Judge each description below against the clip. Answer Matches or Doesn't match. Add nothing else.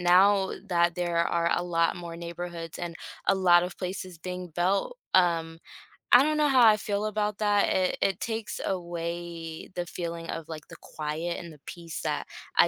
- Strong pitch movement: Doesn't match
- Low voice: Doesn't match